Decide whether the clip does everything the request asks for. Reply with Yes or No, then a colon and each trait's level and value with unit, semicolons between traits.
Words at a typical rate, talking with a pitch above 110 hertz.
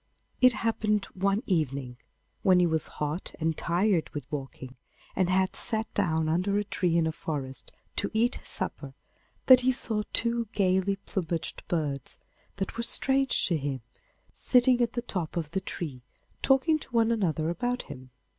Yes: average, 165 wpm; medium, 185 Hz